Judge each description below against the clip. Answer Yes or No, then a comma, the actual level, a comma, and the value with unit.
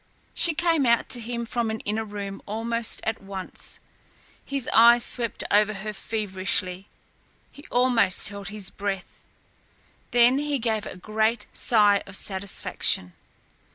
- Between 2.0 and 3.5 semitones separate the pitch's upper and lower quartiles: Yes, average, 3.0 semitones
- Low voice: No, high, 220 Hz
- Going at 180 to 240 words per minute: No, slow, 135 wpm